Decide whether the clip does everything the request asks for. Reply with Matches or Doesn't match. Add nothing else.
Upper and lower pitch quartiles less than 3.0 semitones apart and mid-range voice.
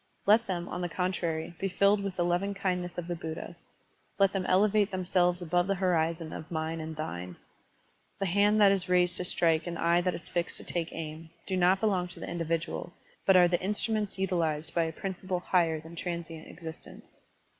Matches